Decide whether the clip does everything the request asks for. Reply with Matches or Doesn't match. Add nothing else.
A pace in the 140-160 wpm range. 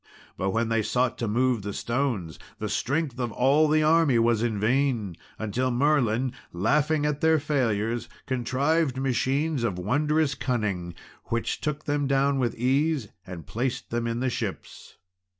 Matches